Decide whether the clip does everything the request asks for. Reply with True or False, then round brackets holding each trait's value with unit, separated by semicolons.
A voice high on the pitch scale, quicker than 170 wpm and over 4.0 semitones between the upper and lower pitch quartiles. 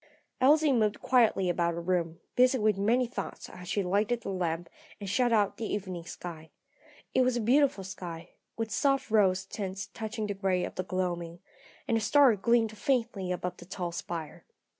True (200 Hz; 185 wpm; 4.5 semitones)